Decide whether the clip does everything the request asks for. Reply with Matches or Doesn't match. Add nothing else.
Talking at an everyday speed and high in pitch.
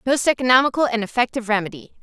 Matches